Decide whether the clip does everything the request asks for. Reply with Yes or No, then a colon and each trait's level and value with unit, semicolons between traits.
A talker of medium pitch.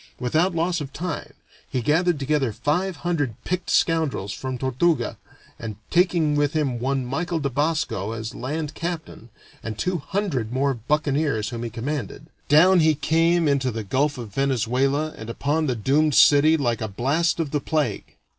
Yes: medium, 145 Hz